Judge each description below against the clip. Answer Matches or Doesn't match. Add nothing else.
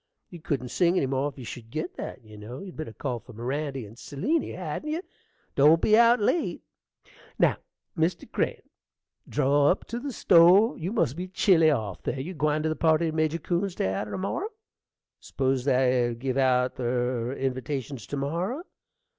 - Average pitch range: Doesn't match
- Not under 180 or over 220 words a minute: Matches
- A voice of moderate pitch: Matches